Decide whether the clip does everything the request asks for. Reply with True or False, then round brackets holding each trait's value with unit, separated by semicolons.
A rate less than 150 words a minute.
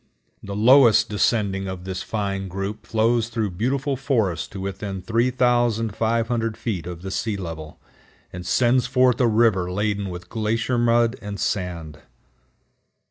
True (135 wpm)